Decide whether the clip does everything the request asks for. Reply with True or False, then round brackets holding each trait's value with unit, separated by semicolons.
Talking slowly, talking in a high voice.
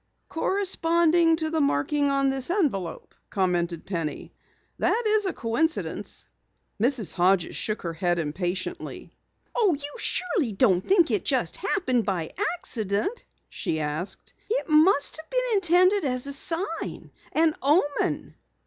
True (130 wpm; 280 Hz)